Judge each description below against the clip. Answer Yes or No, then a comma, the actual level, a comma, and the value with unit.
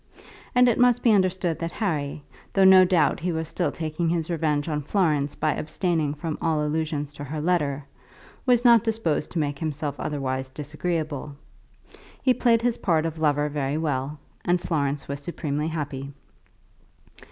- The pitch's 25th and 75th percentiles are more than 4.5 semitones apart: No, average, 3.4 semitones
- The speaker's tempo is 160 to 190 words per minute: Yes, average, 165 wpm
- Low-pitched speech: No, medium, 155 Hz